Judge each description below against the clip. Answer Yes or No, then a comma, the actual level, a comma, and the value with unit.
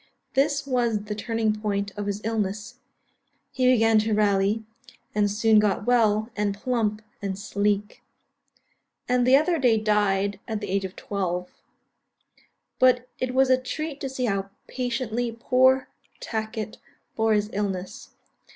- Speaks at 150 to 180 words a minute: No, average, 140 wpm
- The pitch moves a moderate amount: Yes, average, 3.3 semitones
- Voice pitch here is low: No, high, 215 Hz